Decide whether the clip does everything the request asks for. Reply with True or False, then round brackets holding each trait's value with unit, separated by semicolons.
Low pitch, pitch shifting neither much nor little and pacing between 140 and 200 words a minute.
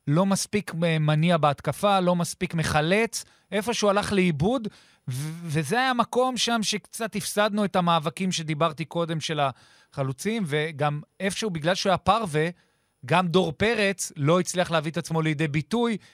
False (180 Hz; 4.2 semitones; 150 wpm)